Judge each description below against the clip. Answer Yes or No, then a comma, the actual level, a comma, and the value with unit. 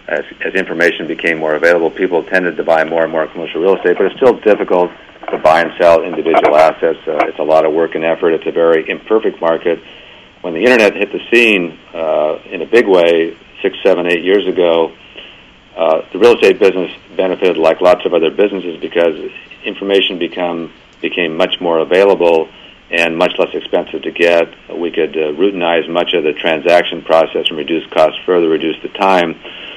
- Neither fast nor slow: Yes, average, 190 wpm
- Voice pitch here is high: No, very low, 95 Hz